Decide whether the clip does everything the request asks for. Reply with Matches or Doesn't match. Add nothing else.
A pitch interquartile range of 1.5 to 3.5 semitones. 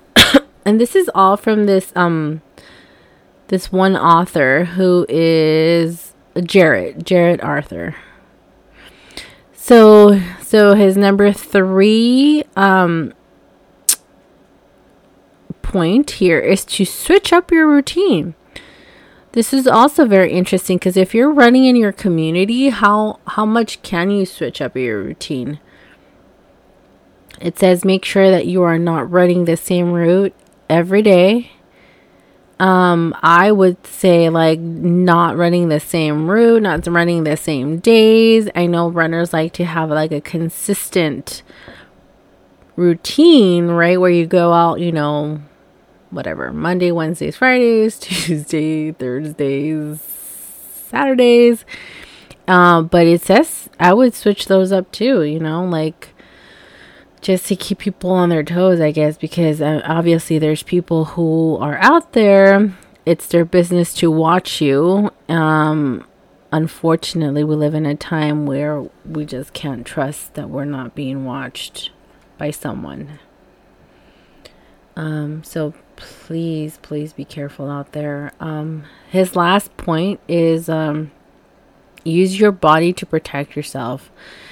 Doesn't match